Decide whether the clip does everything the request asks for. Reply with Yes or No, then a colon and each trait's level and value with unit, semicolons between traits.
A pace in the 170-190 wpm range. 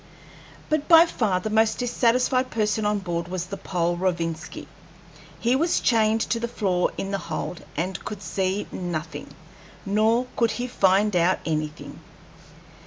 No: average, 150 wpm